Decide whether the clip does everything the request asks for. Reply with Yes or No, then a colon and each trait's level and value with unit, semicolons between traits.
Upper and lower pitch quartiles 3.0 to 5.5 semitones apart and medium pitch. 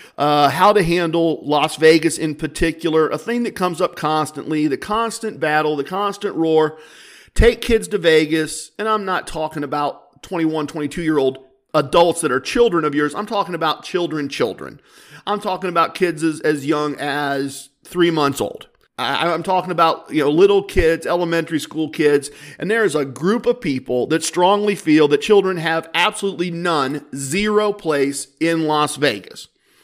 Yes: average, 3.8 semitones; medium, 160 Hz